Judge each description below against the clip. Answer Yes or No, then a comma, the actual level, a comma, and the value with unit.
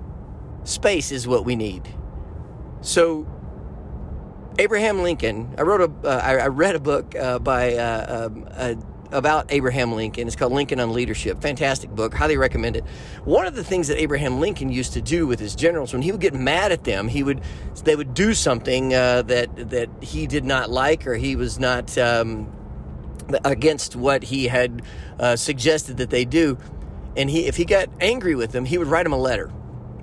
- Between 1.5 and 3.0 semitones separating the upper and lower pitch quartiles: No, average, 4.1 semitones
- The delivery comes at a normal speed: Yes, average, 190 wpm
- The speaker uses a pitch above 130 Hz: No, low, 125 Hz